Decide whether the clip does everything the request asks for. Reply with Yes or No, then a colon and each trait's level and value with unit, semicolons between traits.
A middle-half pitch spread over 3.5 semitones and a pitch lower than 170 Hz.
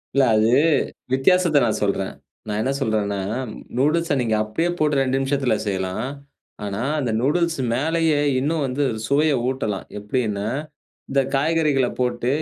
Yes: wide, 5.4 semitones; low, 135 Hz